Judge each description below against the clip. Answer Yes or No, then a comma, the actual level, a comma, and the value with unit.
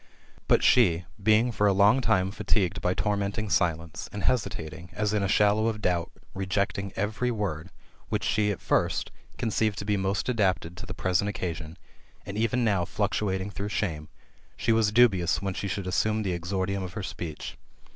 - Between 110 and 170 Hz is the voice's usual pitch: No, low, 100 Hz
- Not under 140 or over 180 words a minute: Yes, average, 175 wpm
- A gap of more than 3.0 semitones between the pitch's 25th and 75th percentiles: No, narrow, 2.5 semitones